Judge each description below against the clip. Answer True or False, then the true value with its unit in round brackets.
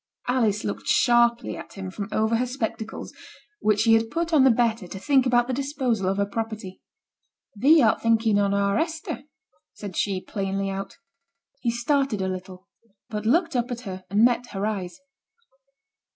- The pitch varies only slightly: False (3.8 semitones)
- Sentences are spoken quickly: False (175 wpm)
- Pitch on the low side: False (225 Hz)